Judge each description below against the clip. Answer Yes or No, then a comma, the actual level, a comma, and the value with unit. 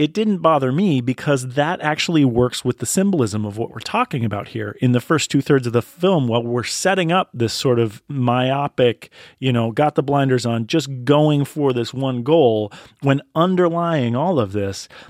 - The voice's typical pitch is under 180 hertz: Yes, low, 135 Hz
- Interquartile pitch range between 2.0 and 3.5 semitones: No, average, 4.3 semitones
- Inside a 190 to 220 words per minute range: Yes, average, 200 wpm